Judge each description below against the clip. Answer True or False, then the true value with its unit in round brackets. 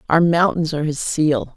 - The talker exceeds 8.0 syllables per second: False (5.1 syllables/s)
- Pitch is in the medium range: True (155 Hz)